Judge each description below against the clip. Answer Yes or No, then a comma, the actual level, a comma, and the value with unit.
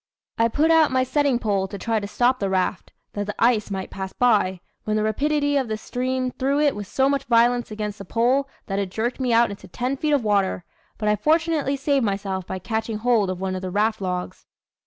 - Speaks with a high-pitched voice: Yes, high, 225 Hz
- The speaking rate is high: Yes, fast, 230 wpm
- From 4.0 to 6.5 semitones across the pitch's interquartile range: Yes, average, 4.8 semitones